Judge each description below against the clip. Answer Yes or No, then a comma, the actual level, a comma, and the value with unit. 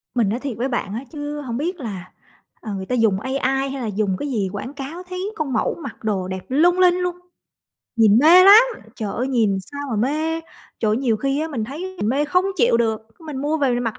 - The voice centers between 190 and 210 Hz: No, very high, 265 Hz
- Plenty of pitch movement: Yes, wide, 5.7 semitones